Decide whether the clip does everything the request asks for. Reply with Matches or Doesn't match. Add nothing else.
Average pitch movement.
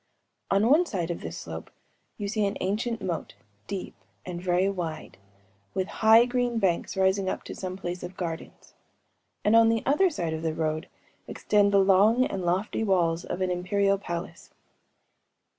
Matches